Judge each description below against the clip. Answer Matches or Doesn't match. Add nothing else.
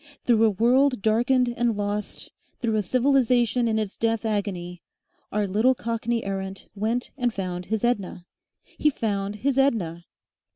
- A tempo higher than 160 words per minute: Doesn't match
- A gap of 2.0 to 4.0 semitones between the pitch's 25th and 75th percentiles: Matches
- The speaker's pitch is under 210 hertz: Doesn't match